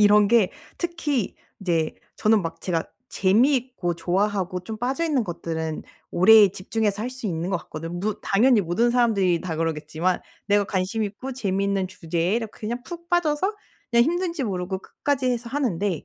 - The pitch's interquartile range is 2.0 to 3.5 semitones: No, average, 5.3 semitones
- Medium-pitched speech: No, high, 205 Hz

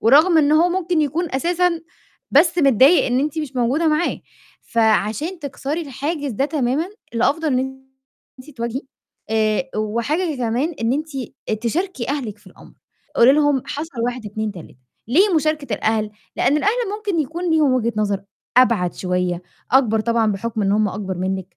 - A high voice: Yes, very high, 265 Hz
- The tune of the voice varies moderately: No, wide, 5.9 semitones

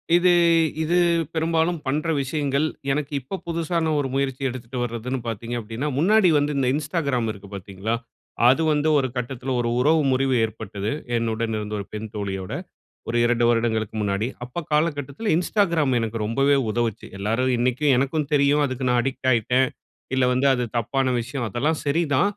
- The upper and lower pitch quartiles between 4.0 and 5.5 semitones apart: Yes, average, 4.4 semitones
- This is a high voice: No, low, 130 Hz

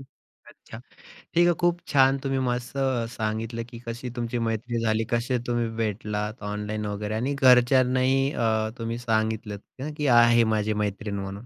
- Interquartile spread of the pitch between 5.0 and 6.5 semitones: No, average, 2.9 semitones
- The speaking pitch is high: No, low, 115 Hz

